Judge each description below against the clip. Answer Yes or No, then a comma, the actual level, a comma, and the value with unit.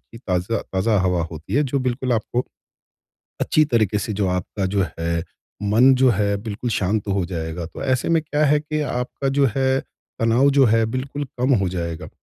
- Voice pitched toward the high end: No, low, 115 Hz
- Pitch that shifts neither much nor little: No, wide, 6.0 semitones